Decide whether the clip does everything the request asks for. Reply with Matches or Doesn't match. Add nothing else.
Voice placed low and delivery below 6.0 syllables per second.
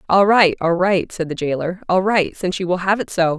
Doesn't match